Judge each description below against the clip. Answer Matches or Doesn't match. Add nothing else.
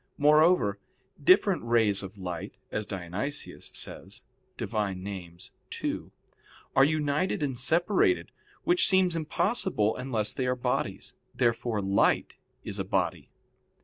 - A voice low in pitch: Matches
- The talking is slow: Matches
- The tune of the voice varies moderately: Doesn't match